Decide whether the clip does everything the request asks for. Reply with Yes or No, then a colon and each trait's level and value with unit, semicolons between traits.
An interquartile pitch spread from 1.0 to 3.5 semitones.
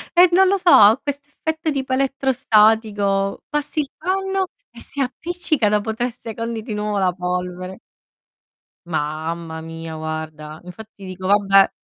No: wide, 7.5 semitones